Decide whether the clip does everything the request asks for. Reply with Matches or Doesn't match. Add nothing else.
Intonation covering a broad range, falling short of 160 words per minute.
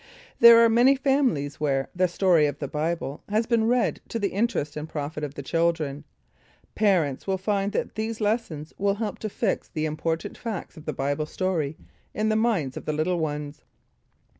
Doesn't match